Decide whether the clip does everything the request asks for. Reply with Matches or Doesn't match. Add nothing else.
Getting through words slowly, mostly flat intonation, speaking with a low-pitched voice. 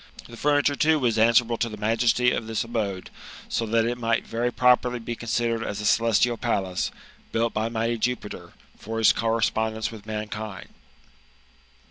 Doesn't match